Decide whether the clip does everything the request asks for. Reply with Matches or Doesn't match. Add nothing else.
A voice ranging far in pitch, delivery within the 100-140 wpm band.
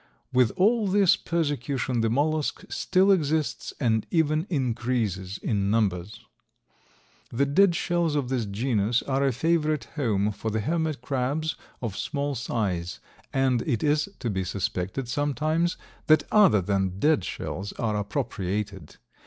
Matches